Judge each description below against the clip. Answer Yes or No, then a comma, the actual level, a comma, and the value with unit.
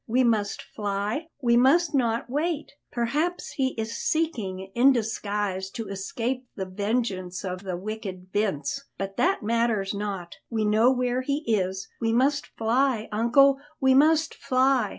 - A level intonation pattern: No, average, 4.8 semitones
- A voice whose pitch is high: Yes, high, 230 Hz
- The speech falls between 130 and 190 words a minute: Yes, average, 150 wpm